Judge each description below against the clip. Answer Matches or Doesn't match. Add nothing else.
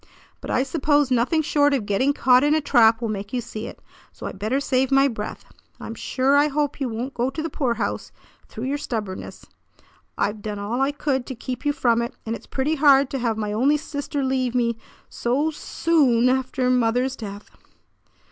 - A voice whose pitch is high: Matches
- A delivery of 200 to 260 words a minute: Matches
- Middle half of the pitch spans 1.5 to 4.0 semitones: Matches